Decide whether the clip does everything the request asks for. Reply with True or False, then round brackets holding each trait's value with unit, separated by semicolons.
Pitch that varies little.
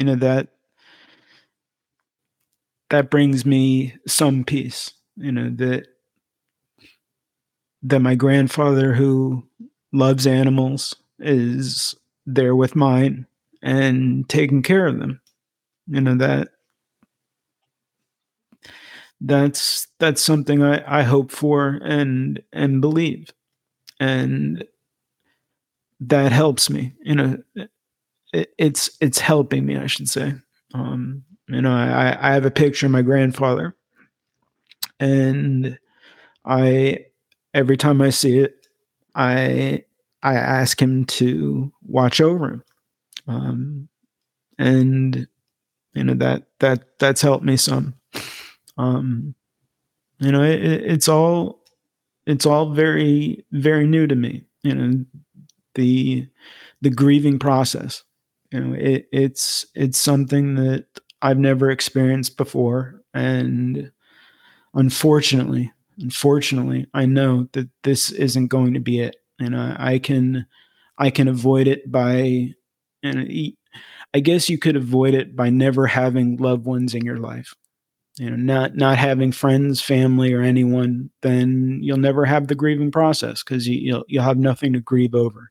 True (1.9 semitones)